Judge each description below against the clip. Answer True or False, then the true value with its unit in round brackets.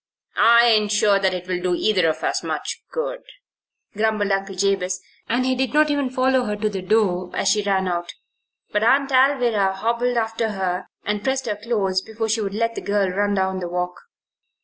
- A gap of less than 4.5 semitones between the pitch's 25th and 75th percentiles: True (3.6 semitones)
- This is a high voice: True (210 Hz)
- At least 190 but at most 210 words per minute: True (195 wpm)